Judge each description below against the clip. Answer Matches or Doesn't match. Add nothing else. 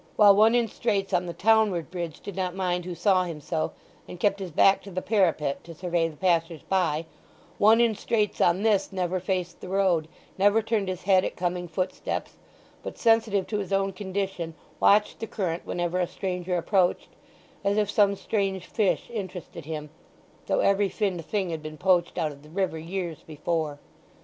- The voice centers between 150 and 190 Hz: Matches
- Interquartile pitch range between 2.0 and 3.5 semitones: Matches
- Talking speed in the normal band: Matches